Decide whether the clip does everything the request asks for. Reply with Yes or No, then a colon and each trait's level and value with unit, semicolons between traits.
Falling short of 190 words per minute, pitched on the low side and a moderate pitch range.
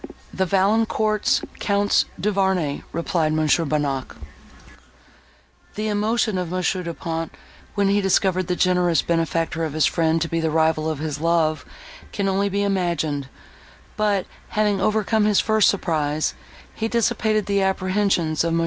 No: average, 145 wpm; medium, 180 Hz; average, 3.9 semitones